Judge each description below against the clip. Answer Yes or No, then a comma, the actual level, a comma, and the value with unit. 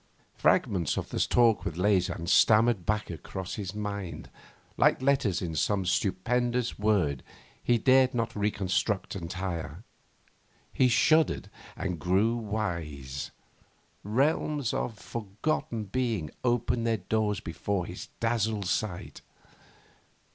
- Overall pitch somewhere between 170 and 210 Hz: No, low, 105 Hz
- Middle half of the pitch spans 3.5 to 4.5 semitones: Yes, average, 4.2 semitones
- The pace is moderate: No, slow, 110 wpm